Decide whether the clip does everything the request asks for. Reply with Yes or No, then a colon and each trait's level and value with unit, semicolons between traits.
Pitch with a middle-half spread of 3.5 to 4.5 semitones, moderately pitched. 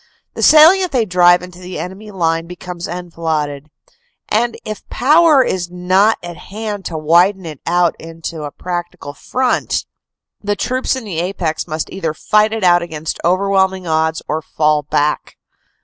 Yes: average, 4.0 semitones; medium, 180 Hz